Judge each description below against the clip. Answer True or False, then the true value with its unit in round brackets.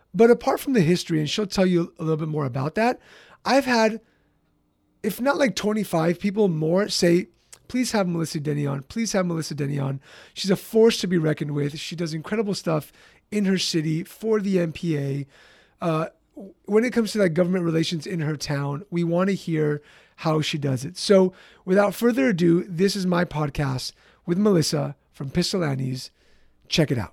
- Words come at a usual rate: True (185 wpm)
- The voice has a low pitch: False (175 Hz)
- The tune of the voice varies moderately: True (4.6 semitones)